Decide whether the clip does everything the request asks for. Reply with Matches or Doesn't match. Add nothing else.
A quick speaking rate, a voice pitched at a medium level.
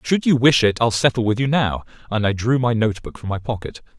Doesn't match